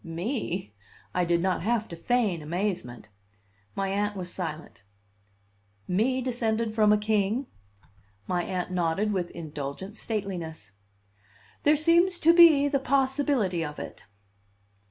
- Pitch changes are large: Yes, wide, 6.1 semitones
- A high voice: Yes, high, 200 Hz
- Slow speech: Yes, slow, 130 wpm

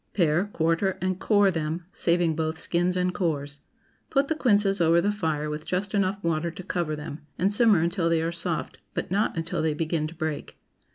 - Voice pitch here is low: No, medium, 170 Hz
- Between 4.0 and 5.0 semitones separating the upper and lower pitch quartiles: No, average, 3.1 semitones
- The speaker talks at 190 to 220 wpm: Yes, average, 195 wpm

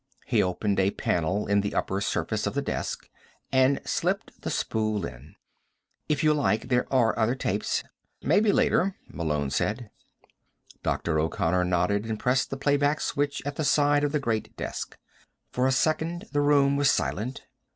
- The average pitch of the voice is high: No, low, 125 Hz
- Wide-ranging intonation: Yes, wide, 6.2 semitones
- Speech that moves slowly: No, average, 170 wpm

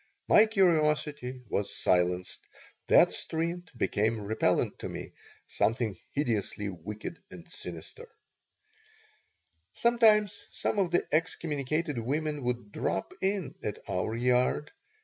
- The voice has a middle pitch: Yes, medium, 145 Hz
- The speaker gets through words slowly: Yes, slow, 110 wpm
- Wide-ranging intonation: Yes, wide, 7.6 semitones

